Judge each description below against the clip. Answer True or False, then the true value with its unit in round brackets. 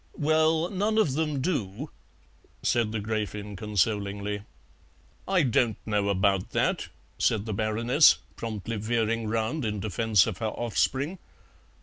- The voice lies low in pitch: True (110 Hz)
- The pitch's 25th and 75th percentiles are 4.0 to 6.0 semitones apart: True (5.1 semitones)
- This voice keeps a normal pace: False (125 wpm)